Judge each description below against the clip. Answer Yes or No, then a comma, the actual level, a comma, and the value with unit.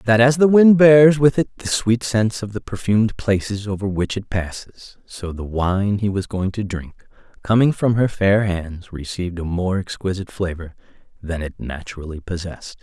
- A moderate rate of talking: Yes, average, 185 wpm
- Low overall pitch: Yes, low, 105 Hz